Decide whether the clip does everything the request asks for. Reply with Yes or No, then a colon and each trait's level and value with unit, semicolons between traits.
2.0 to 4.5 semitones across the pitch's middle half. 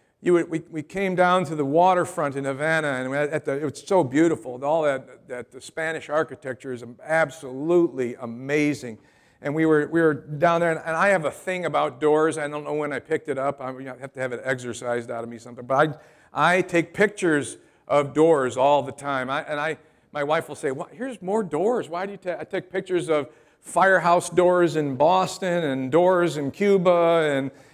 Yes: average, 3.7 semitones